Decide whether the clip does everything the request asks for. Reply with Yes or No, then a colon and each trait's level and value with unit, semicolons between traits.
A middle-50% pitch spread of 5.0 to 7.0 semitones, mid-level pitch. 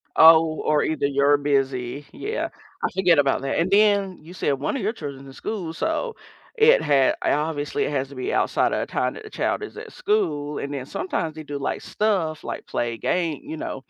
Yes: average, 5.3 semitones; medium, 155 Hz